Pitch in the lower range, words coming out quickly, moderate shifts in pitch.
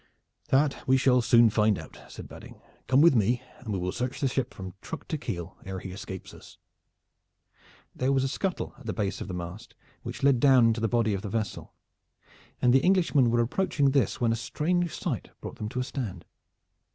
Yes: low, 120 Hz; fast, 210 wpm; average, 4.4 semitones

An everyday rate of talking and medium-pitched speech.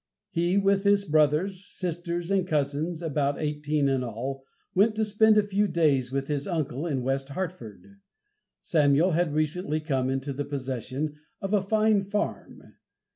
Yes: average, 155 wpm; medium, 155 Hz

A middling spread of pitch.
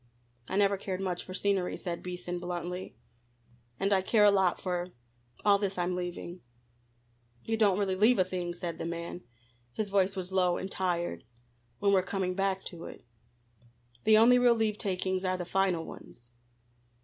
No: narrow, 1.9 semitones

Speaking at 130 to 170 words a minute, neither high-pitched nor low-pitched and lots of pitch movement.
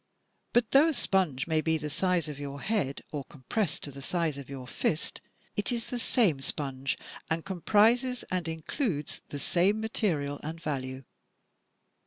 Yes: average, 165 wpm; medium, 160 Hz; wide, 6.5 semitones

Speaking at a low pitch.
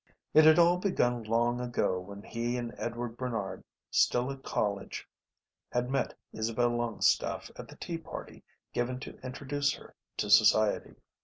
Yes: low, 120 Hz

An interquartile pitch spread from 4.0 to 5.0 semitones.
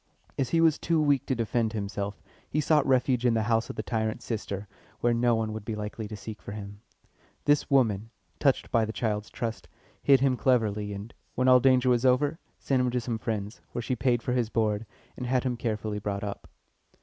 No: average, 3.1 semitones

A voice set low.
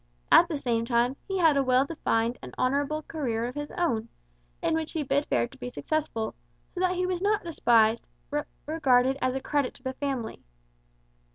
No: very high, 275 Hz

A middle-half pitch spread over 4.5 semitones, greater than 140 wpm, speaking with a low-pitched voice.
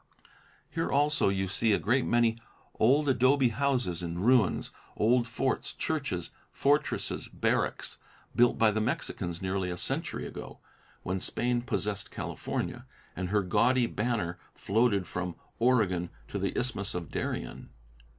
No: average, 5.2 semitones; slow, 135 wpm; low, 110 Hz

